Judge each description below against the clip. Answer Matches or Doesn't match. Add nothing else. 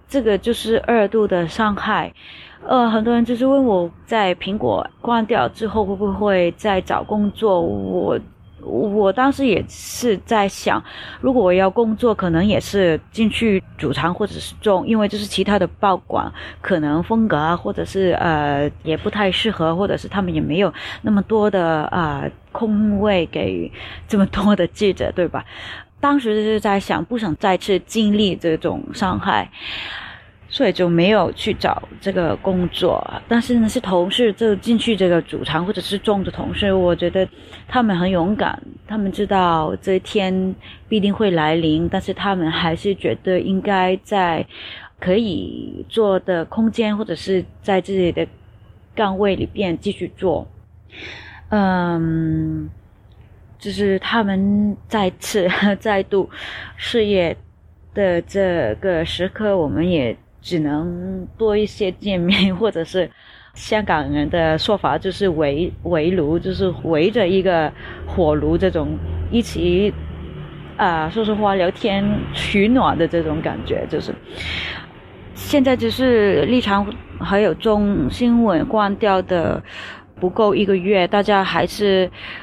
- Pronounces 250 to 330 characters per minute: Doesn't match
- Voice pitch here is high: Matches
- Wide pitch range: Doesn't match